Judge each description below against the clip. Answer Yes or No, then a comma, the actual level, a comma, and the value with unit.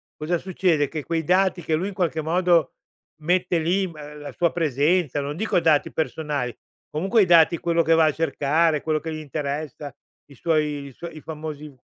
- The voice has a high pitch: No, medium, 160 Hz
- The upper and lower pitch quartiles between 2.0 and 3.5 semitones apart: Yes, narrow, 2.4 semitones